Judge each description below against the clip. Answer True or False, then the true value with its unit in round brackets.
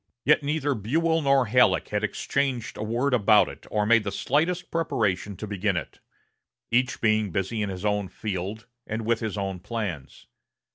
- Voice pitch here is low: True (110 Hz)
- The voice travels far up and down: False (4.2 semitones)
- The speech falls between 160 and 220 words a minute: True (175 wpm)